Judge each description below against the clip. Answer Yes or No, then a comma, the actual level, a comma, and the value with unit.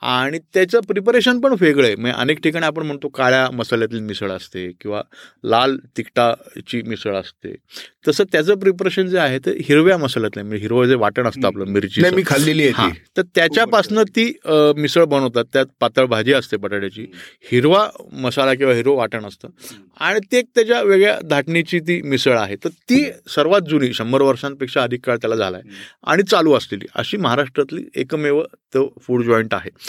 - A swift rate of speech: Yes, fast, 165 wpm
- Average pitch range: No, wide, 6.9 semitones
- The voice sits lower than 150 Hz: Yes, low, 135 Hz